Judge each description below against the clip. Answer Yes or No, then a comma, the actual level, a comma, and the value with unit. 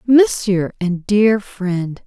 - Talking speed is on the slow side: Yes, slow, 115 wpm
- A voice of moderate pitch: No, high, 200 Hz